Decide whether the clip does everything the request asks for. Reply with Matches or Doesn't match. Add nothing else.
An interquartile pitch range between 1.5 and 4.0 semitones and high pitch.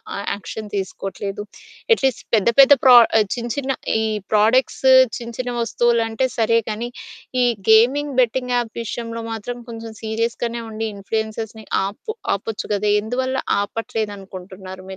Matches